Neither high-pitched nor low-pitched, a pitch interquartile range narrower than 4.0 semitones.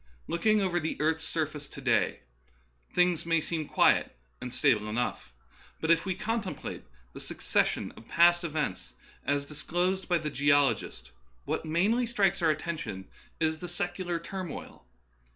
Yes: medium, 165 Hz; average, 3.6 semitones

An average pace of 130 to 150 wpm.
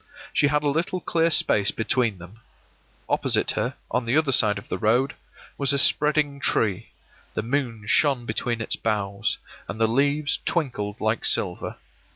No: average, 165 wpm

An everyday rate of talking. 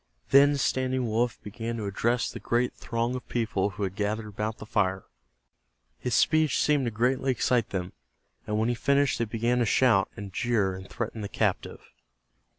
Yes: average, 180 wpm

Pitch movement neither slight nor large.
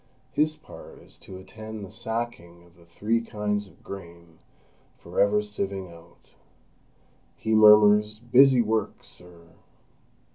Yes: average, 3.8 semitones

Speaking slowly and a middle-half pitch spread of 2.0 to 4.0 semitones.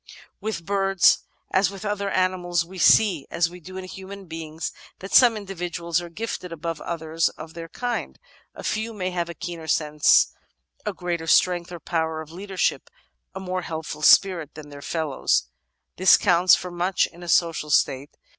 No: average, 170 wpm; average, 2.7 semitones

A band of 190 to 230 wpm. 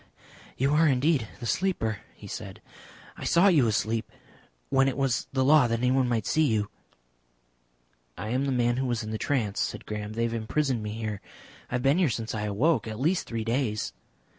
Yes: average, 200 wpm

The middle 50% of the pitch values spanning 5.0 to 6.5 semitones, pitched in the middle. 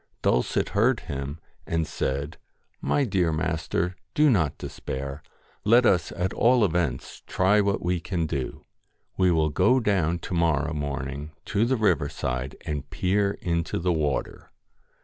No: average, 5.3 semitones; very low, 85 Hz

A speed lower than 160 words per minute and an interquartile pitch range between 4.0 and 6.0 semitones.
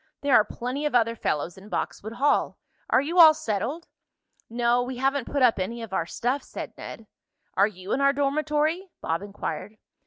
No: average, 185 wpm; average, 5.1 semitones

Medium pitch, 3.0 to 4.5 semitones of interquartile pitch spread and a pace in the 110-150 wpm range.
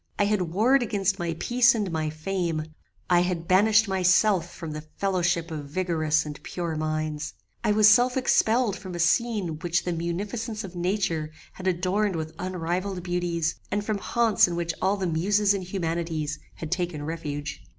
No: medium, 180 Hz; average, 3.6 semitones; average, 170 wpm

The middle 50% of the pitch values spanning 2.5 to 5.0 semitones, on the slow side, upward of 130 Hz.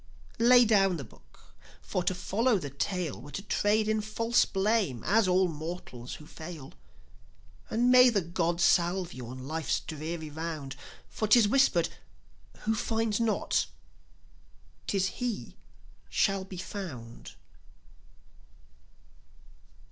No: wide, 5.4 semitones; slow, 125 wpm; medium, 185 Hz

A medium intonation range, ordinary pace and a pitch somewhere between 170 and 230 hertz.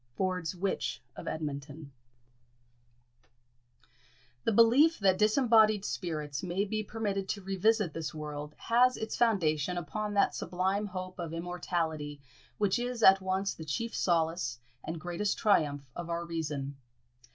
No: average, 4.7 semitones; slow, 130 wpm; medium, 185 Hz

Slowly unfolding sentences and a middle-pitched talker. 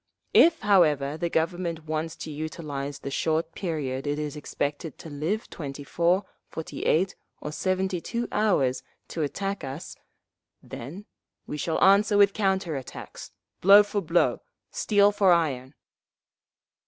Yes: slow, 130 wpm; medium, 165 Hz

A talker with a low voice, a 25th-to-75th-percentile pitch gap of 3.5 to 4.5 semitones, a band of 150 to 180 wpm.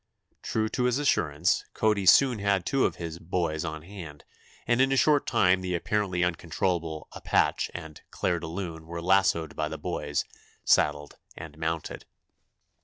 Yes: very low, 85 Hz; average, 4.0 semitones; average, 160 wpm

